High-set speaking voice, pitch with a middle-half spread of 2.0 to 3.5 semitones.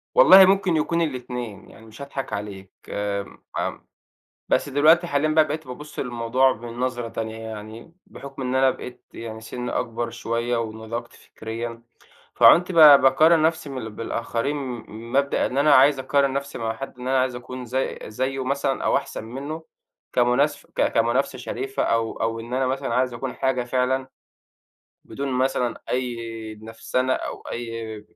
No: low, 125 Hz; average, 3.2 semitones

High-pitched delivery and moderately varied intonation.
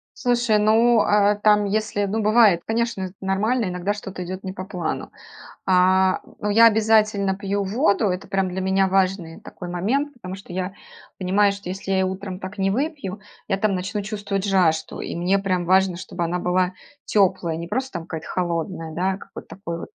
No: high, 195 Hz; narrow, 2.3 semitones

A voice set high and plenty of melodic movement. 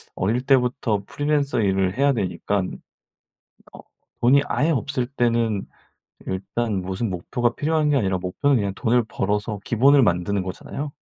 No: low, 115 Hz; wide, 6.0 semitones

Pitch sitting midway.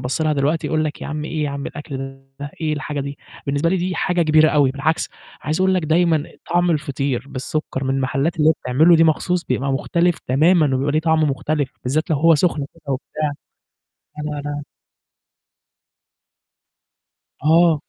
Yes: medium, 150 Hz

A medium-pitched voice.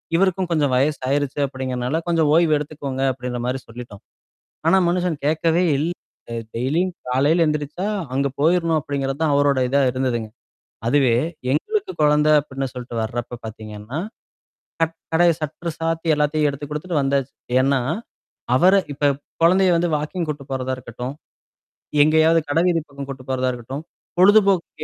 Yes: medium, 145 Hz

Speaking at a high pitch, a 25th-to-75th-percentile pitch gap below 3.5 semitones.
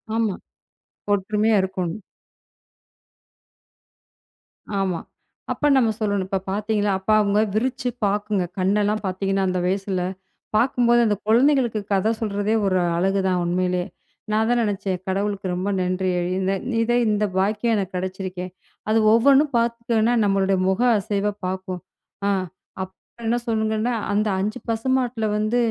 Yes: high, 205 Hz; average, 2.9 semitones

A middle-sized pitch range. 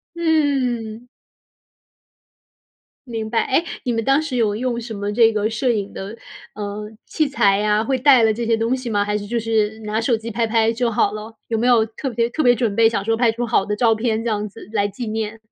No: narrow, 2.2 semitones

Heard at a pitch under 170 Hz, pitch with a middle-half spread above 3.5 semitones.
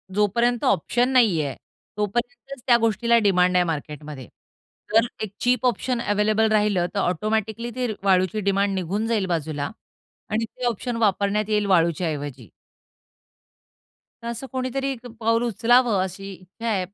No: high, 210 Hz; average, 4.2 semitones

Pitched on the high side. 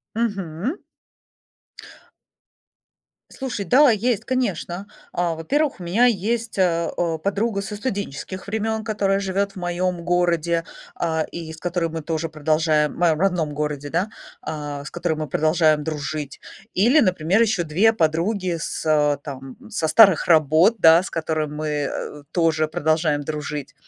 No: medium, 170 Hz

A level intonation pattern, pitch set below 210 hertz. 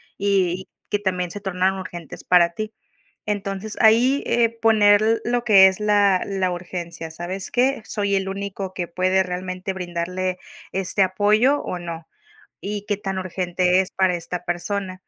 Yes: narrow, 2.2 semitones; high, 190 Hz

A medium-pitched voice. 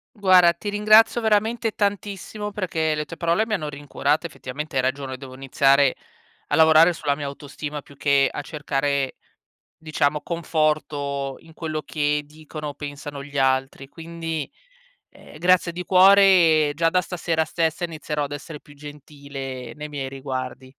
Yes: medium, 150 Hz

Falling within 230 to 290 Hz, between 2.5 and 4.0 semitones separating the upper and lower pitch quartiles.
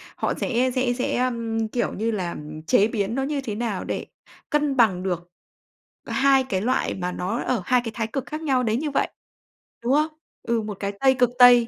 Yes: high, 235 Hz; average, 3.6 semitones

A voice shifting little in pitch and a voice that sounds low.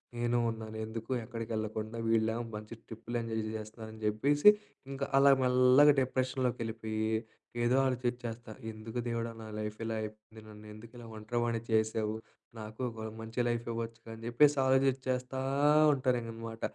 Yes: narrow, 2.2 semitones; low, 115 Hz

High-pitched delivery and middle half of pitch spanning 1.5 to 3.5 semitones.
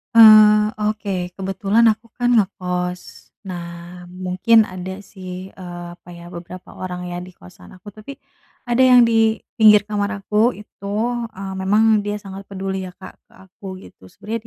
Yes: high, 195 Hz; average, 2.8 semitones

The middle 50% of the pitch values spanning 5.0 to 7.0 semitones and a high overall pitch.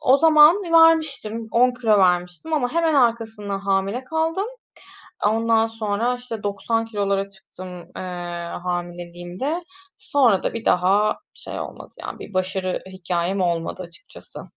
Yes: average, 5.3 semitones; high, 210 Hz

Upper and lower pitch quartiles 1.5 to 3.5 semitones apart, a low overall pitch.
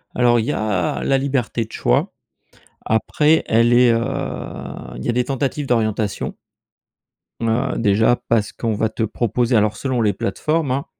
Yes: average, 2.8 semitones; low, 115 Hz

